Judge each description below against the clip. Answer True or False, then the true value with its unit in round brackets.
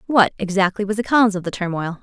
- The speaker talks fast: True (235 wpm)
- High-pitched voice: True (200 Hz)